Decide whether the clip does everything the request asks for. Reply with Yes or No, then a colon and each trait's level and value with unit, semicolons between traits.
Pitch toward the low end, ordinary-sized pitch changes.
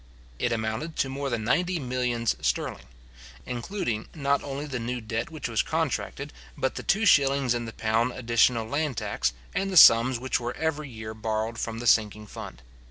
Yes: low, 120 Hz; average, 3.7 semitones